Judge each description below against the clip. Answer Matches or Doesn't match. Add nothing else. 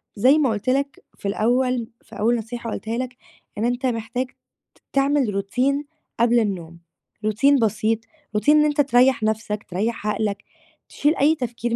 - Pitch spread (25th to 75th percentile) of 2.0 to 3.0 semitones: Doesn't match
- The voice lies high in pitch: Matches